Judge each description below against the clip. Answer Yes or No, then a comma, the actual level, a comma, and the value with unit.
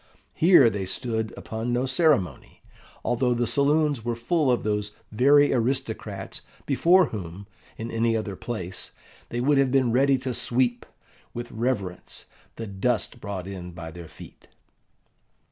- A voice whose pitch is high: No, low, 120 Hz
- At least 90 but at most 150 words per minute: Yes, average, 145 wpm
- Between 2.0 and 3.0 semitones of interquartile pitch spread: No, average, 4.1 semitones